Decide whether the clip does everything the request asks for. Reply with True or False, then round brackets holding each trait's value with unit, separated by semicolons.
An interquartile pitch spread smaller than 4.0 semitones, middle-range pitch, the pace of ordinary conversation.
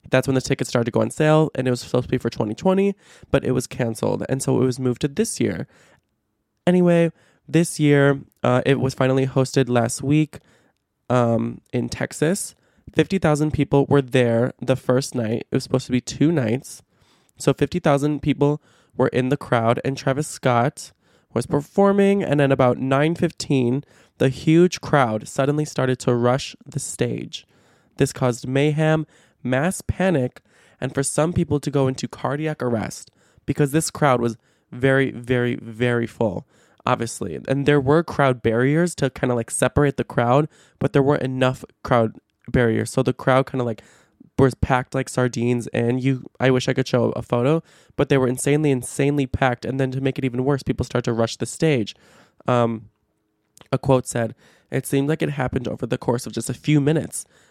False (2.9 semitones; 130 Hz; 185 wpm)